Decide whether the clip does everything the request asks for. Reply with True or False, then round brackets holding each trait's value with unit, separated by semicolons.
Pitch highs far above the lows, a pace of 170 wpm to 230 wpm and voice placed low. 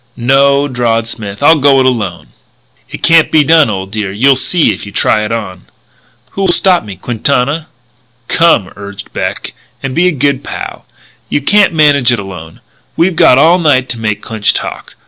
True (6.2 semitones; 180 wpm; 130 Hz)